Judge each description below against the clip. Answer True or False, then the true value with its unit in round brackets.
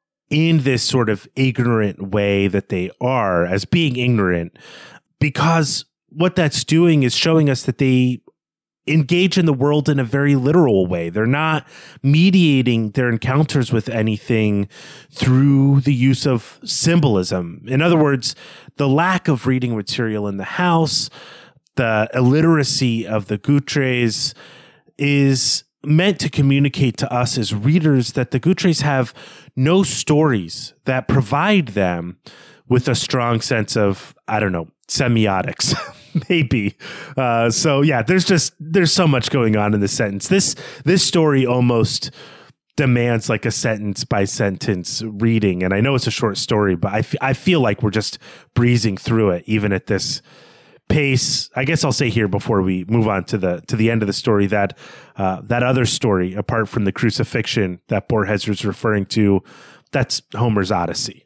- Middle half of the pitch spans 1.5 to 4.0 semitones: False (5.2 semitones)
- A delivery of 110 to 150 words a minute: False (160 wpm)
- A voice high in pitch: False (125 Hz)